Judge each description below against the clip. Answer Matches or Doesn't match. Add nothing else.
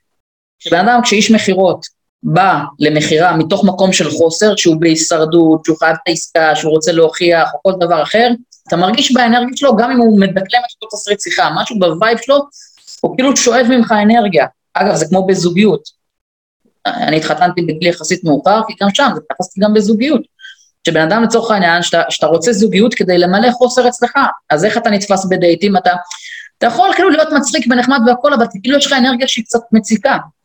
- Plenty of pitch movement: Matches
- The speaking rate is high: Matches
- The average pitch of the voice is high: Matches